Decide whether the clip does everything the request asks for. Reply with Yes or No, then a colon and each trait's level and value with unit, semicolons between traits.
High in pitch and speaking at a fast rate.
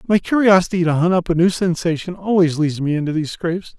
No: medium, 175 Hz; fast, 220 wpm